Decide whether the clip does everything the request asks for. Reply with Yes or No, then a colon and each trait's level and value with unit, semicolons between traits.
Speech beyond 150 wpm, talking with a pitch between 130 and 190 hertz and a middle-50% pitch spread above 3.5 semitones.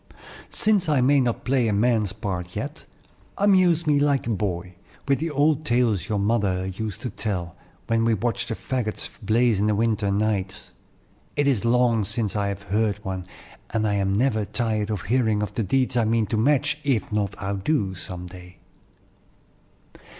No: average, 175 wpm; low, 110 Hz; average, 3.9 semitones